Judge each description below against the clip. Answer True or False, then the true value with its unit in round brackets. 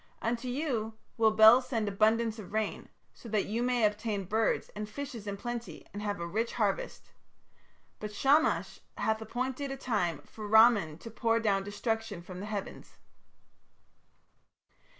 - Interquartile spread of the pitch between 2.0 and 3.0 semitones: True (2.4 semitones)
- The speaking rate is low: False (150 wpm)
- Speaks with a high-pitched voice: True (220 Hz)